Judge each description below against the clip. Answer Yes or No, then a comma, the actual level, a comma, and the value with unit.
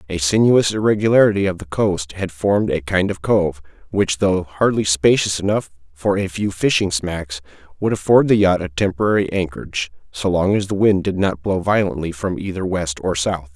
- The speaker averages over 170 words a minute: Yes, average, 190 wpm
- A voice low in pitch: Yes, very low, 90 Hz